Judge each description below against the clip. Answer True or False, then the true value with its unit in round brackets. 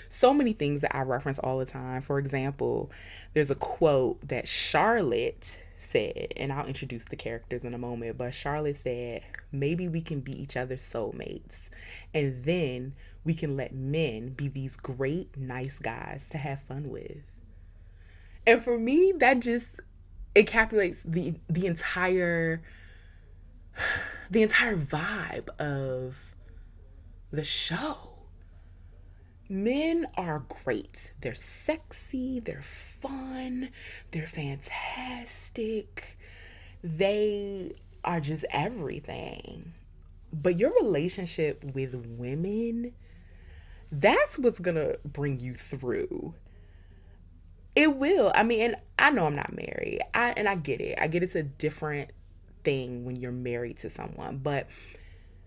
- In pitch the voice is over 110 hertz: True (140 Hz)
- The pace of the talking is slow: True (125 wpm)